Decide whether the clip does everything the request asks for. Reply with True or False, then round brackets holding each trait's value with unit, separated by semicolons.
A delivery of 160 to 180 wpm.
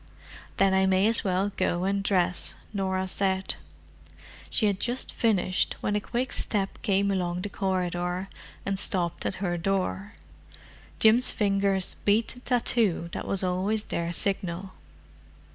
False (145 wpm)